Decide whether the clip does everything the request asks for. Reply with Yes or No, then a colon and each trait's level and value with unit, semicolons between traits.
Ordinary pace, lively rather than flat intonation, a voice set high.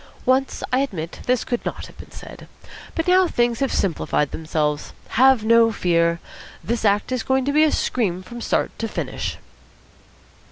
Yes: average, 170 wpm; wide, 6.6 semitones; high, 230 Hz